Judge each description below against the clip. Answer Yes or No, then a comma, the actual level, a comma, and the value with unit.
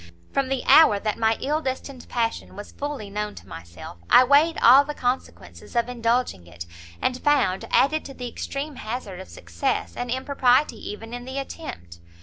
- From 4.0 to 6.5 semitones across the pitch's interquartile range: Yes, average, 4.9 semitones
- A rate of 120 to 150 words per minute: No, average, 175 wpm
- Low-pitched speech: No, high, 245 Hz